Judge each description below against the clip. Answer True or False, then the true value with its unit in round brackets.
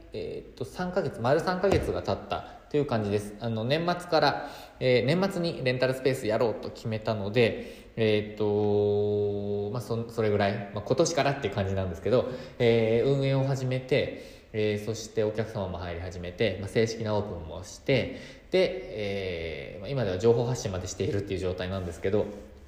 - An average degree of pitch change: True (4.2 semitones)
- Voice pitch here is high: False (110 Hz)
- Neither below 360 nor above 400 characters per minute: True (370 characters per minute)